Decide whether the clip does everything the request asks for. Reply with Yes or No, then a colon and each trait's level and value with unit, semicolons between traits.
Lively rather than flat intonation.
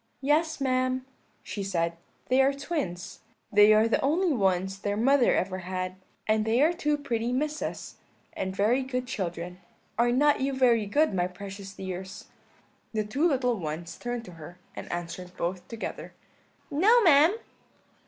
Yes: wide, 6.6 semitones